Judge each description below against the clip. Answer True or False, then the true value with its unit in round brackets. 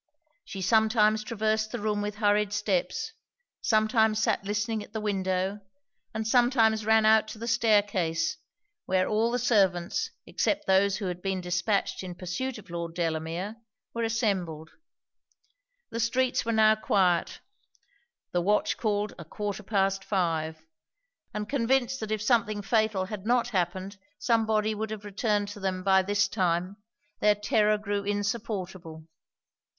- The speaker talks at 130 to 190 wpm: True (150 wpm)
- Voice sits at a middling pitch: False (210 Hz)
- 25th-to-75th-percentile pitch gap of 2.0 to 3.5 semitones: True (2.6 semitones)